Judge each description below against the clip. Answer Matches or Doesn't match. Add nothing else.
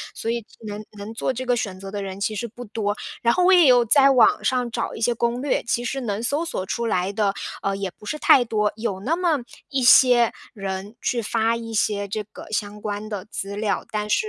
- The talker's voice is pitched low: Doesn't match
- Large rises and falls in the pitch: Doesn't match